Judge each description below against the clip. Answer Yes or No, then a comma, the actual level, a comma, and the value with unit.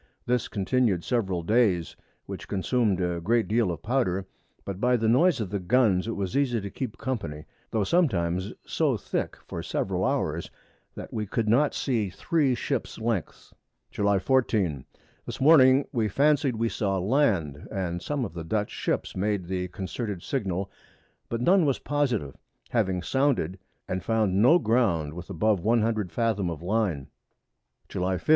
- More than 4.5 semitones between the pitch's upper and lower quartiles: Yes, average, 5.1 semitones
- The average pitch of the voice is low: Yes, low, 105 Hz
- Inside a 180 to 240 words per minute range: No, average, 160 wpm